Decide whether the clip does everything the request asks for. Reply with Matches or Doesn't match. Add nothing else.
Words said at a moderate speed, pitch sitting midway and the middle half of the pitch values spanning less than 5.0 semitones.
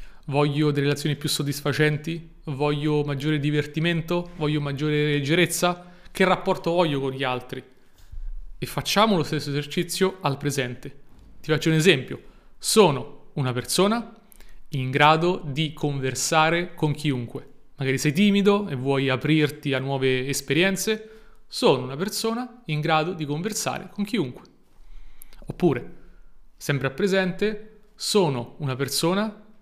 Matches